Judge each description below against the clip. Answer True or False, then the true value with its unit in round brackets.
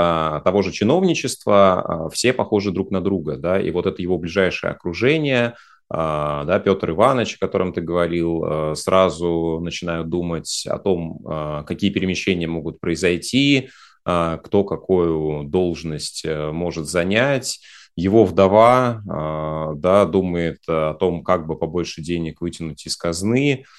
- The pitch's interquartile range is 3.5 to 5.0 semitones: False (3.1 semitones)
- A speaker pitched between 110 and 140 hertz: False (85 Hz)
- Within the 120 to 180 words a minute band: True (125 wpm)